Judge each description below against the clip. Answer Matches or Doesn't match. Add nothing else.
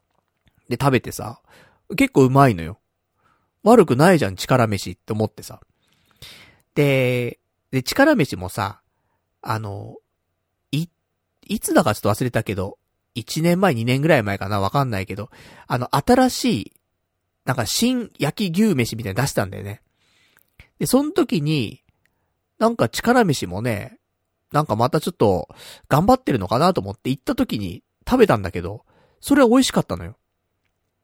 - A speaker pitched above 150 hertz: Doesn't match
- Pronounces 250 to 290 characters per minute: Matches